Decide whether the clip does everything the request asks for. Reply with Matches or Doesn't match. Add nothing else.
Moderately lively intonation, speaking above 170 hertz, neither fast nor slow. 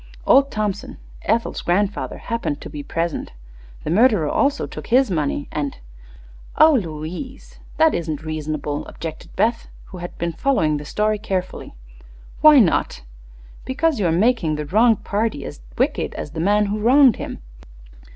Doesn't match